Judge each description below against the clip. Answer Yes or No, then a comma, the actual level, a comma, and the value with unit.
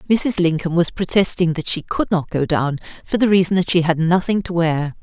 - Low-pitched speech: No, medium, 175 Hz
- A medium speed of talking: No, fast, 225 wpm